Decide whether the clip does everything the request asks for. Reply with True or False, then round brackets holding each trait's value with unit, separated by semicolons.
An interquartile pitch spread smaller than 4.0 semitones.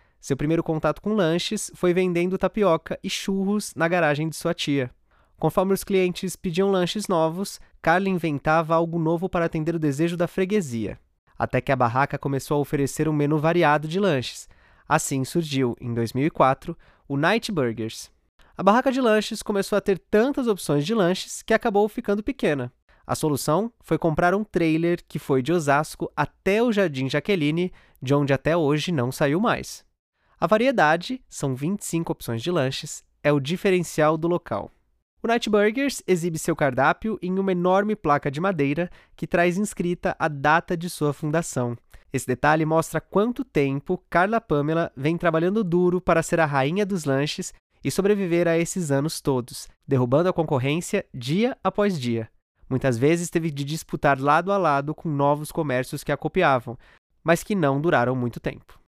False (4.6 semitones)